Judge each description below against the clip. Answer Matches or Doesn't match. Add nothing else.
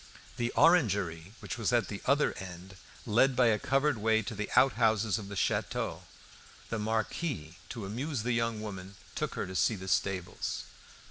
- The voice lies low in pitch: Matches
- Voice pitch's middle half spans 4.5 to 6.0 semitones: Doesn't match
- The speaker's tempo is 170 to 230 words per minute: Matches